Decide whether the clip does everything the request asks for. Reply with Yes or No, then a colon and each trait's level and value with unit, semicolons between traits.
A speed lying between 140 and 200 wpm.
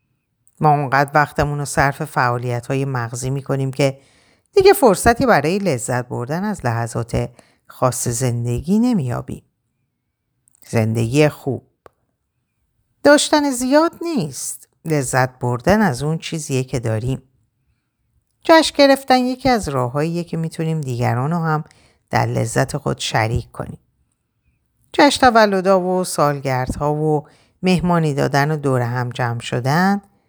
No: average, 120 wpm